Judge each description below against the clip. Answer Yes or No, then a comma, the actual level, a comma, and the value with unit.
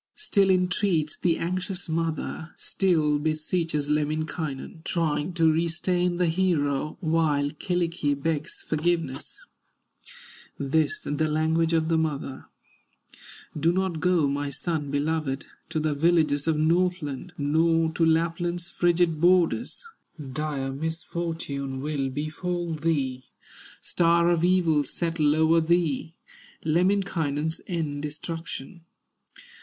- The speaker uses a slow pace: Yes, slow, 105 wpm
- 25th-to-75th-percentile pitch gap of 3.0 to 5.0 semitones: No, narrow, 2.6 semitones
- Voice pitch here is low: No, medium, 160 Hz